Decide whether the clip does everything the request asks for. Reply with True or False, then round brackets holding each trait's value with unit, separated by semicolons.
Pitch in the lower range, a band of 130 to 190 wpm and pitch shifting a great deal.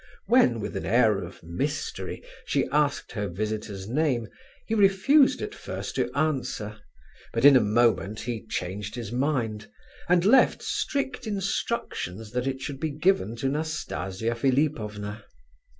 True (120 Hz; 140 wpm; 6.7 semitones)